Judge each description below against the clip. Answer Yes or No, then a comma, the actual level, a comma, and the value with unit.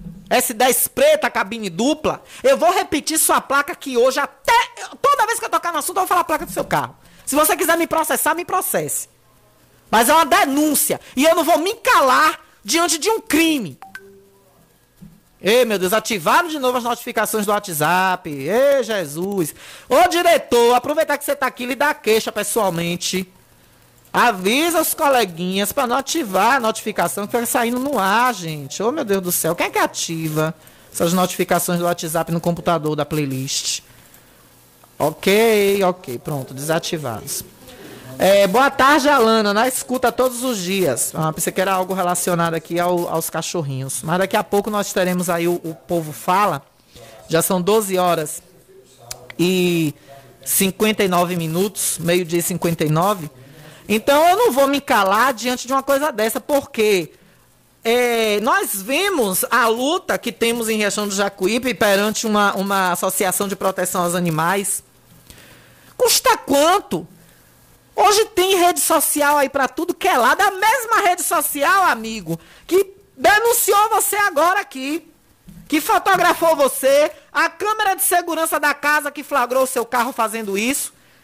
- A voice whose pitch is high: Yes, high, 225 Hz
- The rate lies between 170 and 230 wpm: No, average, 160 wpm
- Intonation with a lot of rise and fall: Yes, wide, 8.9 semitones